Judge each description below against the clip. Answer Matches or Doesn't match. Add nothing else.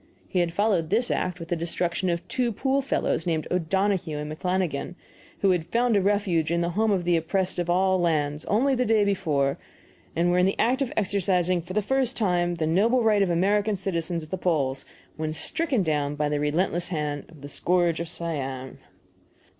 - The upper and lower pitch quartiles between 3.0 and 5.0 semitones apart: Matches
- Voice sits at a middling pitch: Matches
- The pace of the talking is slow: Doesn't match